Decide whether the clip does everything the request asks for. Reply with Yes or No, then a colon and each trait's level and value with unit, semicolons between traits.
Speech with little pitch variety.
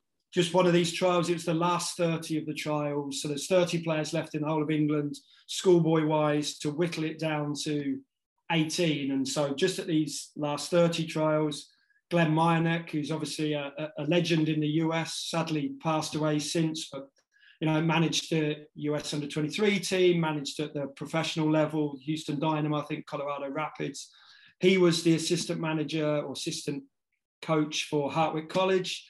Yes: narrow, 2.0 semitones